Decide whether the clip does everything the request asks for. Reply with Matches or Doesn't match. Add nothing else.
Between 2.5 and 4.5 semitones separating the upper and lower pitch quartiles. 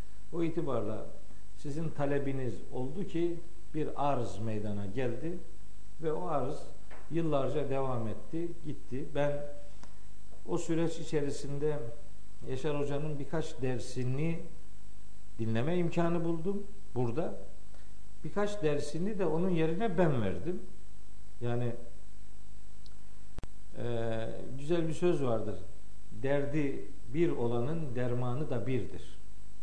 Doesn't match